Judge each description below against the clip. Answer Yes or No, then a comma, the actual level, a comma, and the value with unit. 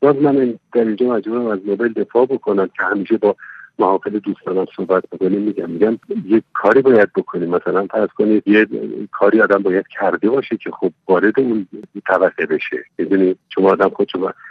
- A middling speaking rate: No, fast, 180 wpm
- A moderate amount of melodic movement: Yes, average, 4.7 semitones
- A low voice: Yes, low, 115 Hz